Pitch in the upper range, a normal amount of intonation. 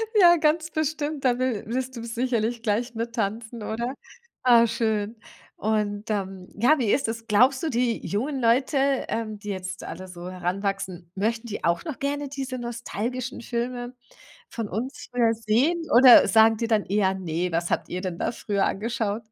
Yes: high, 230 Hz; average, 3.7 semitones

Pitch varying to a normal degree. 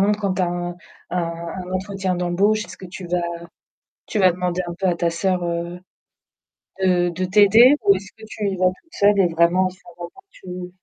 No: narrow, 2.2 semitones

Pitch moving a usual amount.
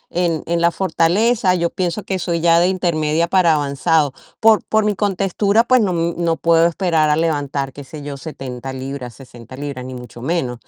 Yes: average, 4.3 semitones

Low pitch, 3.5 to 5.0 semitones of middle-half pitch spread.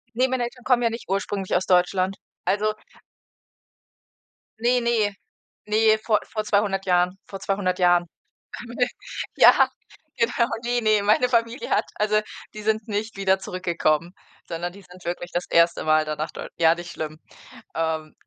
No: high, 195 Hz; average, 4.1 semitones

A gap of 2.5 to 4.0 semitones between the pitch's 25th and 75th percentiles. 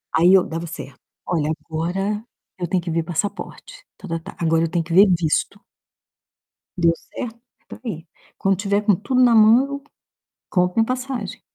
No: average, 4.4 semitones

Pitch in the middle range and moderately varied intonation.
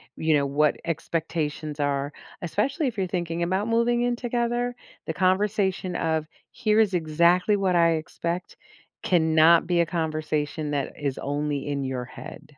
Yes: medium, 170 Hz; average, 4.5 semitones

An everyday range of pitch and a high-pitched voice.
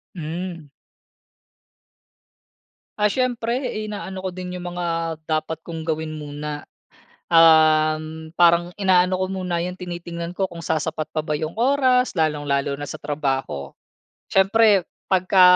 No: average, 3.2 semitones; medium, 170 Hz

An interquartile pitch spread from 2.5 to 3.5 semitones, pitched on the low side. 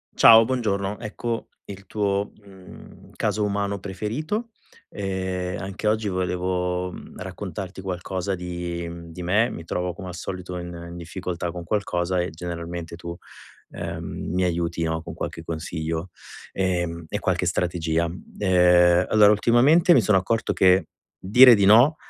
Yes: average, 2.8 semitones; very low, 90 Hz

